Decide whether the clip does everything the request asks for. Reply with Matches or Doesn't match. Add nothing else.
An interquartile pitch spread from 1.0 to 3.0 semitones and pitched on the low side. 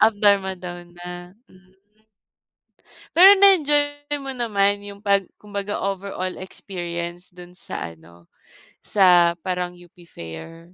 Doesn't match